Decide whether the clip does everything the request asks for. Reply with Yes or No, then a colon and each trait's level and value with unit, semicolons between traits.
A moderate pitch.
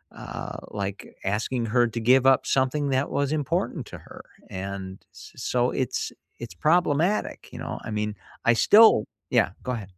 No: low, 120 Hz